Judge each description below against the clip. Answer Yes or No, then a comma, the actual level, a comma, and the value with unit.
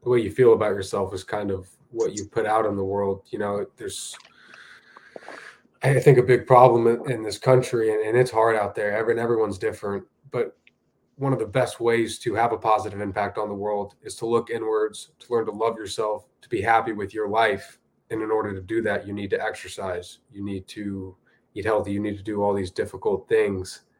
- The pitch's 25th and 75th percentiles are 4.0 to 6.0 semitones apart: No, average, 2.9 semitones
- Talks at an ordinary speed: No, fast, 220 wpm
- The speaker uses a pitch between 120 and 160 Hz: No, low, 110 Hz